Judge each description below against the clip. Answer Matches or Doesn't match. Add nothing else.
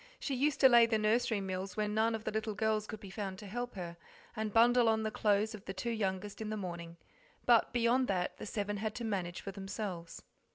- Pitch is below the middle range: Doesn't match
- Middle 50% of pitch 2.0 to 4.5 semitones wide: Matches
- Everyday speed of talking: Doesn't match